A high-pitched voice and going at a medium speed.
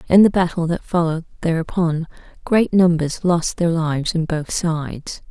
No: medium, 170 Hz; average, 160 wpm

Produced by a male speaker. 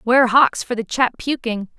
No: female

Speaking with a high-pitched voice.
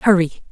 No: medium, 180 Hz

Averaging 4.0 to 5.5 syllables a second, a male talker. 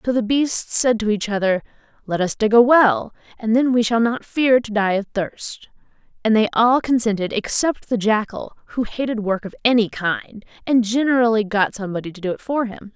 No: 5.1 syllables/s; female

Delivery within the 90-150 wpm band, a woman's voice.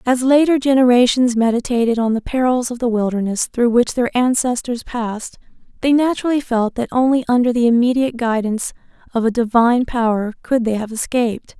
No: average, 165 wpm; female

